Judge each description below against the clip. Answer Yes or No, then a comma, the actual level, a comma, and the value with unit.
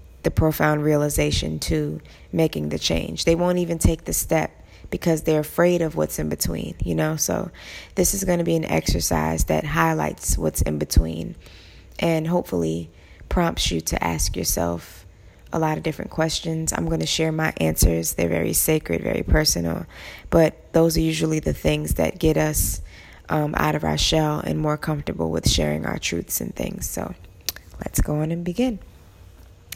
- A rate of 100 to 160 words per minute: No, average, 175 wpm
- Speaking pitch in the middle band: No, very low, 90 Hz